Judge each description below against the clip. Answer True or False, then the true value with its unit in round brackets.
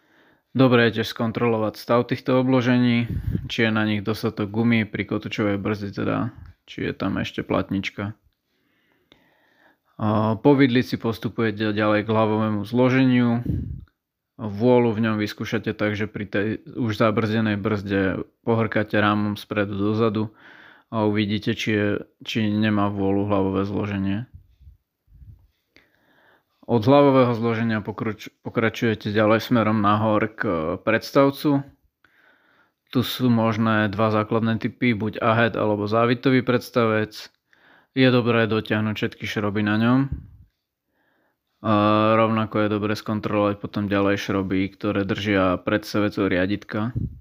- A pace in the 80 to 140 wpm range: True (115 wpm)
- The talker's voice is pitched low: True (110 Hz)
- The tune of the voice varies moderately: False (2.1 semitones)